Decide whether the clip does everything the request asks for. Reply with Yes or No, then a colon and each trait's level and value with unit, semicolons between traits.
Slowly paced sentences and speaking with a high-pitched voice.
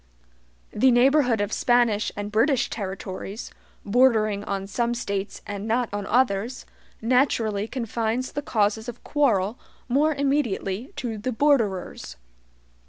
Yes: slow, 120 wpm; high, 225 Hz